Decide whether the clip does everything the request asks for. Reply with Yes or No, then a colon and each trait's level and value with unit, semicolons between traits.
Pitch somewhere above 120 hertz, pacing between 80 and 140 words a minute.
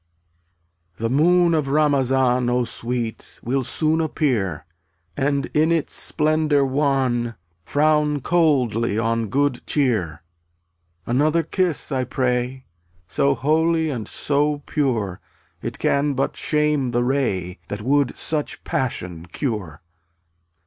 Yes: low, 135 Hz; slow, 135 wpm